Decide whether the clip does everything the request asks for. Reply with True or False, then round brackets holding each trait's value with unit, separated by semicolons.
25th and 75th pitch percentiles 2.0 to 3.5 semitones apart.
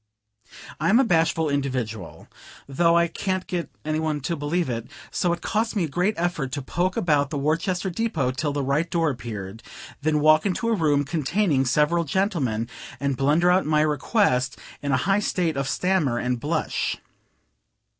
False (4.3 semitones)